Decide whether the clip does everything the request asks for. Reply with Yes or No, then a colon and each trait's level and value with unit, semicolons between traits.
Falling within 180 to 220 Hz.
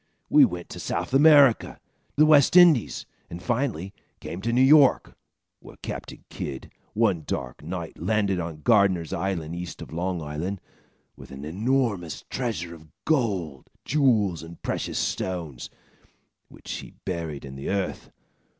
No: very low, 95 Hz